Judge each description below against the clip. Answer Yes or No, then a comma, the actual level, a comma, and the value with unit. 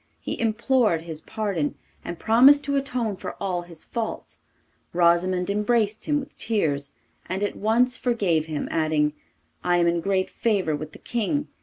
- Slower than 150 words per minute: No, average, 160 wpm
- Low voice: No, high, 200 Hz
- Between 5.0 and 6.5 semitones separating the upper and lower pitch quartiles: Yes, wide, 5.5 semitones